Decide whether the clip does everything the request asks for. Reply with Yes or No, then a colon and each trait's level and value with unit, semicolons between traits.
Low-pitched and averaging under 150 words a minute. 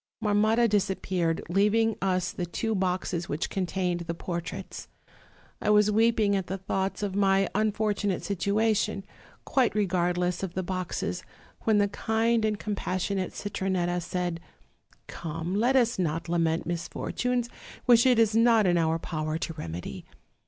No: high, 195 Hz; average, 140 wpm